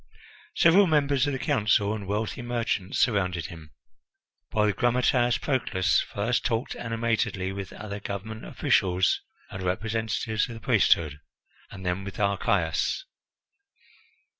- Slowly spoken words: Yes, slow, 125 wpm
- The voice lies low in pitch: Yes, low, 105 Hz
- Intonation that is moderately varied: Yes, average, 3.9 semitones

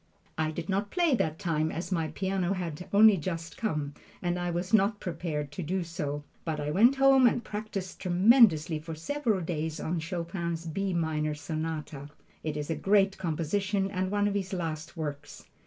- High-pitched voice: No, medium, 175 Hz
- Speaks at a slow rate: No, average, 180 wpm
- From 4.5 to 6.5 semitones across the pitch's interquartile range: No, average, 3.8 semitones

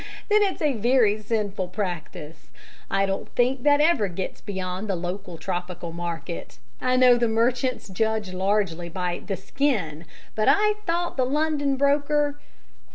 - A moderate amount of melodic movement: No, wide, 6.8 semitones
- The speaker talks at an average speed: Yes, average, 150 wpm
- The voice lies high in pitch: Yes, high, 215 Hz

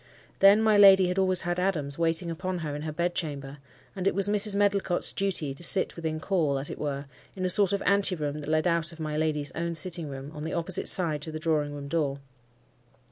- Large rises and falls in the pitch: No, average, 3.8 semitones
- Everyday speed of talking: No, fast, 225 wpm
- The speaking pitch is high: No, medium, 165 Hz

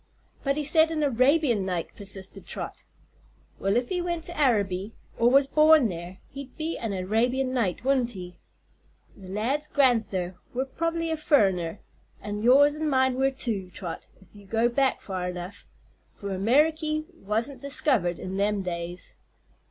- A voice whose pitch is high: Yes, high, 240 Hz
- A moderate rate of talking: Yes, average, 160 wpm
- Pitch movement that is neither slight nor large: No, wide, 6.8 semitones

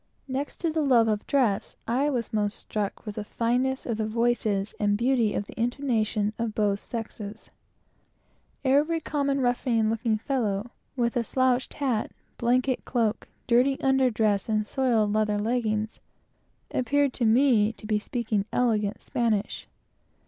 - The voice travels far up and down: No, average, 3.3 semitones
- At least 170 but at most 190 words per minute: No, average, 150 wpm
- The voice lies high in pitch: Yes, high, 230 Hz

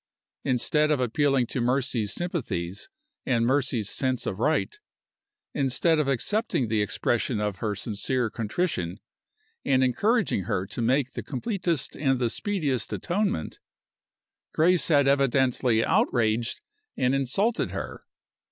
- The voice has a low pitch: Yes, low, 130 Hz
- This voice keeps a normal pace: No, slow, 125 wpm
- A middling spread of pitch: Yes, average, 4.9 semitones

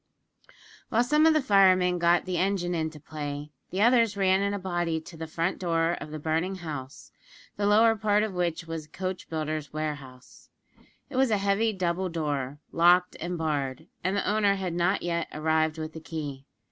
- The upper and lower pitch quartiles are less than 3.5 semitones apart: No, average, 3.9 semitones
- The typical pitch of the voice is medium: Yes, medium, 175 Hz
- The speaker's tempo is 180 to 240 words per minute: Yes, average, 190 wpm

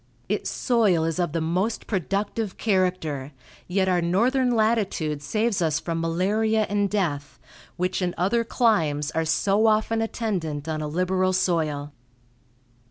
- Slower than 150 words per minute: Yes, average, 140 wpm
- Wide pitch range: No, average, 5.0 semitones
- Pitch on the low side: No, medium, 185 Hz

